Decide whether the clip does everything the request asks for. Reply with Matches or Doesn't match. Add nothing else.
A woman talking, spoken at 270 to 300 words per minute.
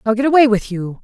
Matches